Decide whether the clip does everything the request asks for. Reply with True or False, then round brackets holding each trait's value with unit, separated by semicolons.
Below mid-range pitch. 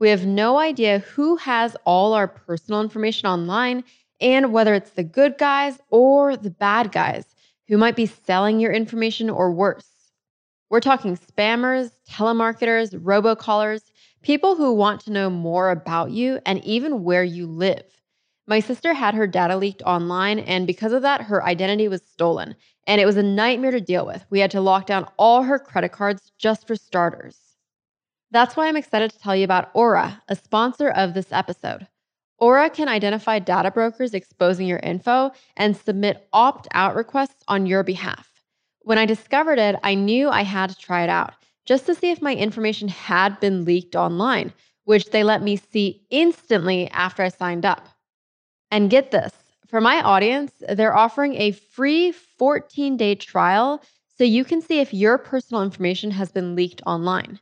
False (215 Hz)